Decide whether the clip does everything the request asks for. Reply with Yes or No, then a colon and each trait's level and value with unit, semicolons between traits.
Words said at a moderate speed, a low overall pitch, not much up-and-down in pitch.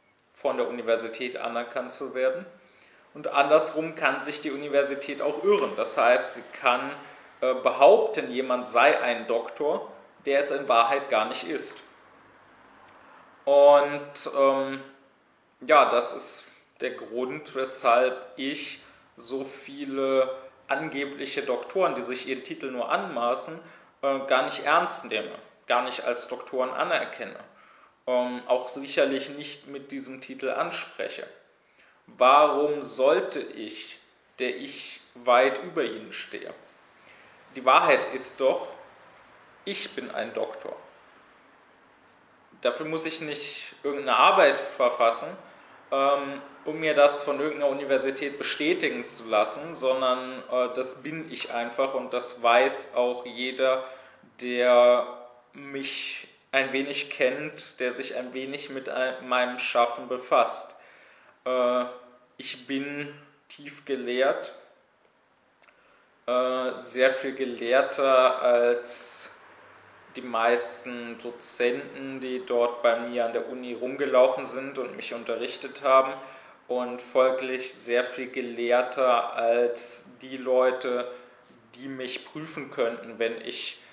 No: slow, 115 wpm; low, 130 Hz; narrow, 2.3 semitones